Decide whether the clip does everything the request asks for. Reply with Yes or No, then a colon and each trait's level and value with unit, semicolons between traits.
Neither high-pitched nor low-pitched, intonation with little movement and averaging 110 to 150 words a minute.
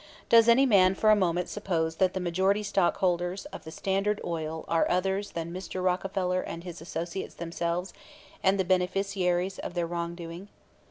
No: medium, 180 Hz; narrow, 2.2 semitones; average, 165 wpm